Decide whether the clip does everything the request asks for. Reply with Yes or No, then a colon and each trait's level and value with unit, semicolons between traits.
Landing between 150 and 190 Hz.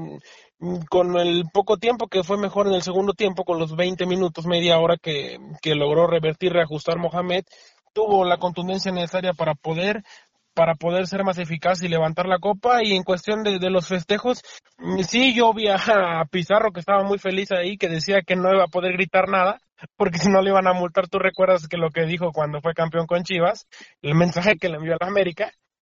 Yes: medium, 185 Hz